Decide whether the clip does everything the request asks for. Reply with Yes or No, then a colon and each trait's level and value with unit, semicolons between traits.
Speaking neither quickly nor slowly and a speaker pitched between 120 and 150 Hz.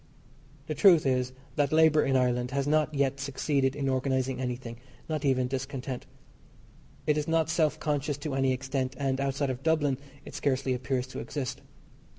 Yes: average, 165 wpm; low, 135 Hz